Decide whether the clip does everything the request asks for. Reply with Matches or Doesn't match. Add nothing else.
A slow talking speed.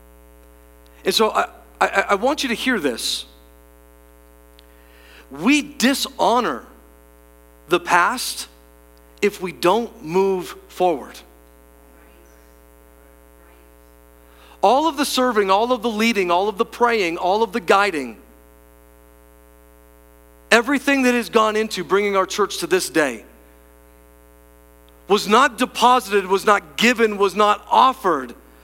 Matches